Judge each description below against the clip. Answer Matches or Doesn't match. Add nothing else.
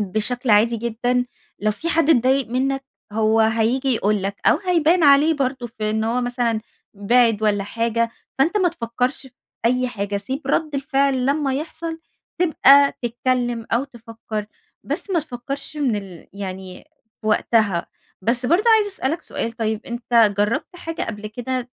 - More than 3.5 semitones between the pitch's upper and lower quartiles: Matches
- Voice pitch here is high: Matches